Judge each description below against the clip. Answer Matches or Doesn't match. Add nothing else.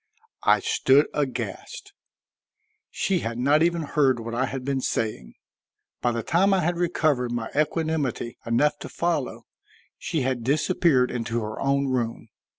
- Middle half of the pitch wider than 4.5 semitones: Matches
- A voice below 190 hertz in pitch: Matches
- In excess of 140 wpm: Matches